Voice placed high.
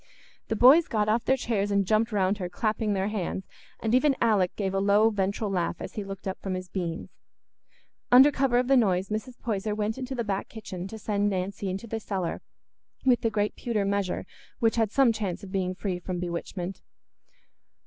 Yes: high, 205 Hz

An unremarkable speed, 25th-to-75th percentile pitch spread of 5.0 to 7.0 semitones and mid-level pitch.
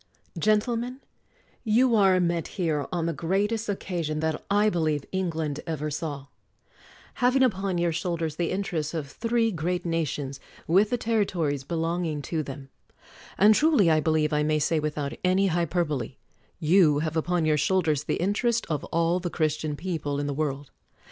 No: average, 165 wpm; average, 4.1 semitones; medium, 165 Hz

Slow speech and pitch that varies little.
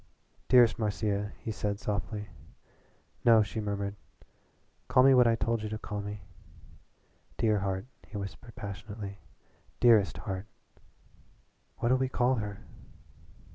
Yes: slow, 125 wpm; narrow, 2.3 semitones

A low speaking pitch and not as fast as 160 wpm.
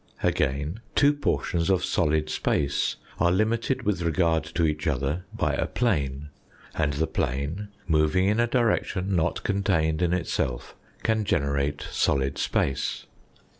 Yes: very low, 80 Hz; slow, 135 wpm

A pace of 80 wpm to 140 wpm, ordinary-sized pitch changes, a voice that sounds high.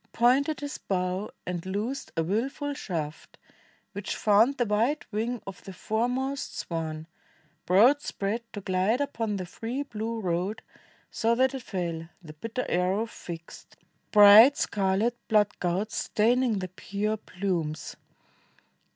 Yes: slow, 135 wpm; average, 4.6 semitones; high, 210 Hz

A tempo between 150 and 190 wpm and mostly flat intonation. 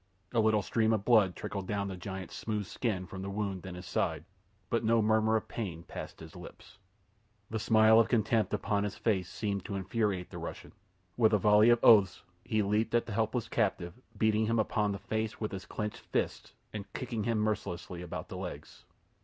No: average, 200 wpm; narrow, 2.1 semitones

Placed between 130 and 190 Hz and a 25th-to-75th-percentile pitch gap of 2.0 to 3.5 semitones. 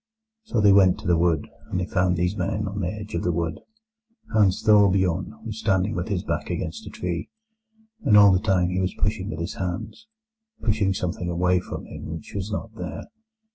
No: very low, 95 Hz; average, 3.1 semitones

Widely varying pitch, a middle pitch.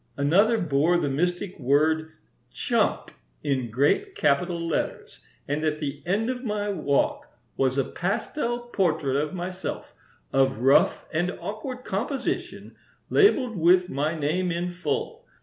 Yes: wide, 6.2 semitones; medium, 175 Hz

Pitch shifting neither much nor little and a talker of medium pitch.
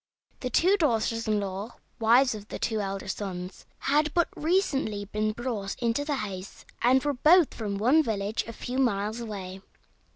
No: average, 4.8 semitones; high, 225 Hz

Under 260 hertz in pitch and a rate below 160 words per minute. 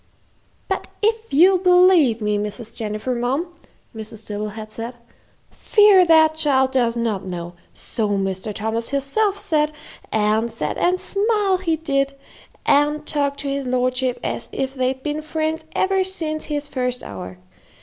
No: very high, 275 Hz; average, 150 wpm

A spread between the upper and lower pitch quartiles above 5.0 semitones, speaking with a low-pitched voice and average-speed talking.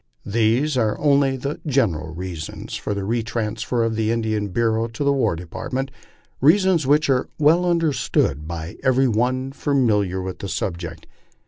Yes: wide, 5.4 semitones; low, 115 Hz; average, 150 wpm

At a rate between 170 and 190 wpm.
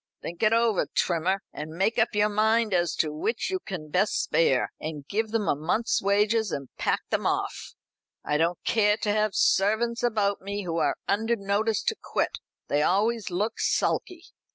Yes: average, 180 wpm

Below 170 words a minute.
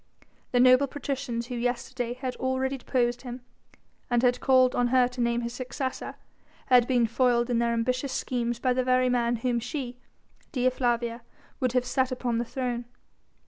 No: average, 175 wpm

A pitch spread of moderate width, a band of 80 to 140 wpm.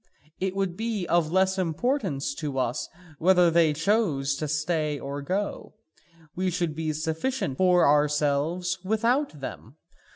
Yes: average, 4.2 semitones; slow, 135 wpm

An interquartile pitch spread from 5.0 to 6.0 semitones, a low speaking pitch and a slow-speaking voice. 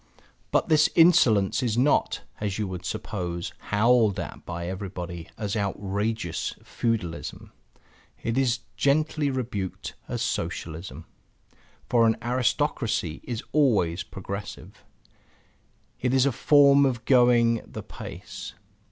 Yes: average, 5.3 semitones; low, 115 Hz; slow, 115 wpm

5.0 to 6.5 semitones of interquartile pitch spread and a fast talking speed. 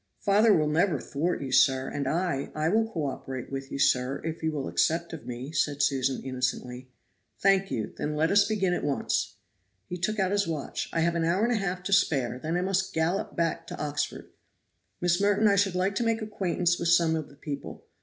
Yes: average, 5.3 semitones; fast, 220 wpm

